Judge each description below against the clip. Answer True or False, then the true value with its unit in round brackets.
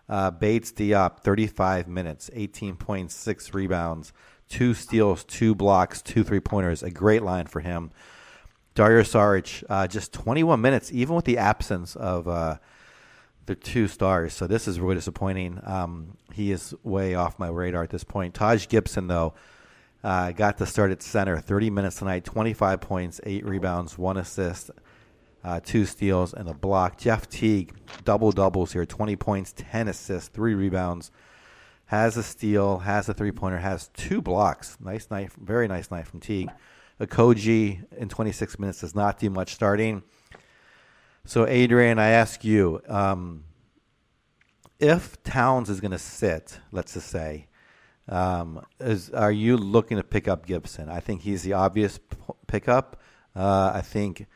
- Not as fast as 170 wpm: True (160 wpm)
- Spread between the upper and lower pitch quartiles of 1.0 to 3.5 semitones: True (3.1 semitones)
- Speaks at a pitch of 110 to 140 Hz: False (100 Hz)